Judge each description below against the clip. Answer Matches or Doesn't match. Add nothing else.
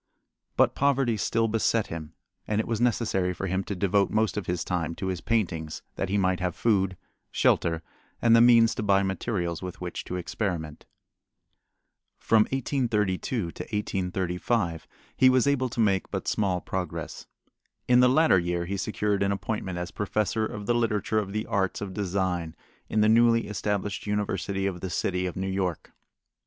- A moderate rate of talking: Matches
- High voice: Doesn't match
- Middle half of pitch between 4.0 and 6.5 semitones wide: Doesn't match